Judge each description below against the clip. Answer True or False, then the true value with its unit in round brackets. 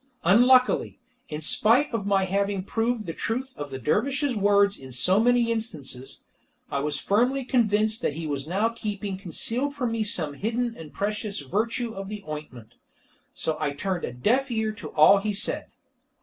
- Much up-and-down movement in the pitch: True (6.4 semitones)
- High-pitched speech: True (205 Hz)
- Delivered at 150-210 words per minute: True (175 wpm)